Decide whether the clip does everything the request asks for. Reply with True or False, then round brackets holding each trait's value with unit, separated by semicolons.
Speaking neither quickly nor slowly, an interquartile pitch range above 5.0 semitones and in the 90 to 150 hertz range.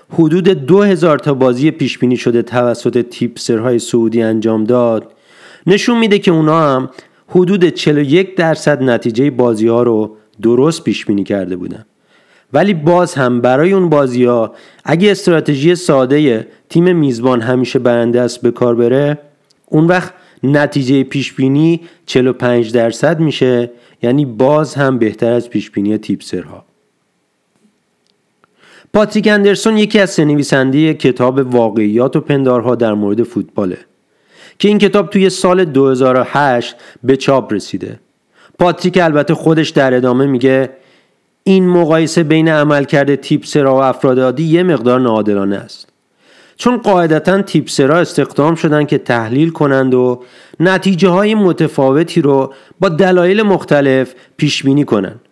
True (135 wpm; 5.6 semitones; 140 Hz)